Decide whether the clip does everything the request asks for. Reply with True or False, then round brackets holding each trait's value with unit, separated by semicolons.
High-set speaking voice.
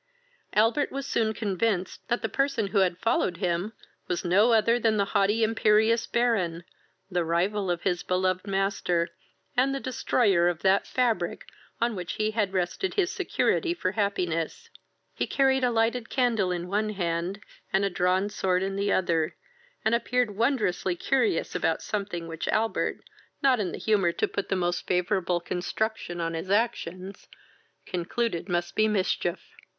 True (200 Hz)